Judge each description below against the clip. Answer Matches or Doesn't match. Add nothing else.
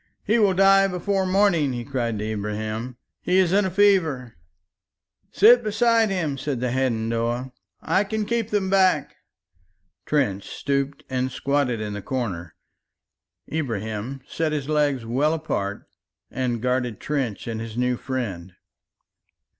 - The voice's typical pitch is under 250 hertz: Matches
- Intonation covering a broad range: Matches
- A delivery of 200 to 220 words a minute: Doesn't match